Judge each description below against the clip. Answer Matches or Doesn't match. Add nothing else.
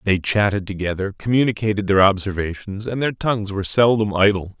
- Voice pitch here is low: Matches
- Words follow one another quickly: Doesn't match